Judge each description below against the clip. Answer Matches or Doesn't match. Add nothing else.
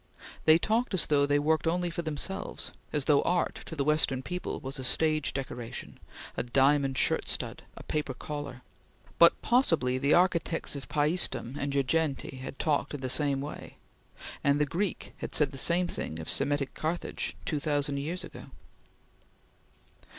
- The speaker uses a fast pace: Doesn't match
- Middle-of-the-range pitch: Matches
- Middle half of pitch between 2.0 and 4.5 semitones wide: Matches